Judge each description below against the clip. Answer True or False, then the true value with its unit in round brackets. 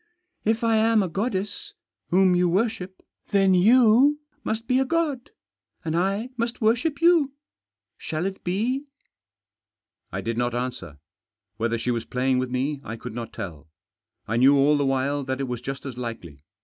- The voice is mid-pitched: True (175 Hz)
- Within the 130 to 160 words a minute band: False (175 wpm)